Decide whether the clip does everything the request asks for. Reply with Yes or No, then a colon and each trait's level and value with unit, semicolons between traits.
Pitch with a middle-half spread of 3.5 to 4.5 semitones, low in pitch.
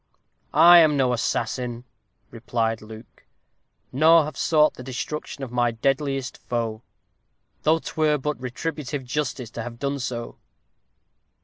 Yes: average, 4.0 semitones; low, 130 Hz